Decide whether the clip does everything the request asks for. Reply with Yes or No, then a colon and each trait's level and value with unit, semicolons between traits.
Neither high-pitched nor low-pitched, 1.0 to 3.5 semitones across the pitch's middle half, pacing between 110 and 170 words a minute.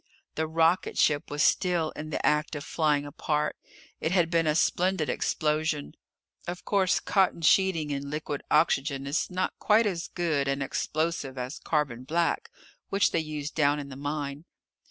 Yes: medium, 155 Hz; average, 2.7 semitones; average, 160 wpm